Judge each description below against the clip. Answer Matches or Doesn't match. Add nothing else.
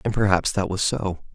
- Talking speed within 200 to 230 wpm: Matches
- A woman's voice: Doesn't match